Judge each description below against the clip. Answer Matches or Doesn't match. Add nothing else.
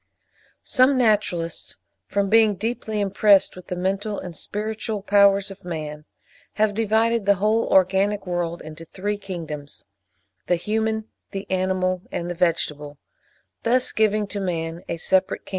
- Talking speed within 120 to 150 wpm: Matches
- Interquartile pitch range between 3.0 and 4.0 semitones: Matches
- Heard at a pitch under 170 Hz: Doesn't match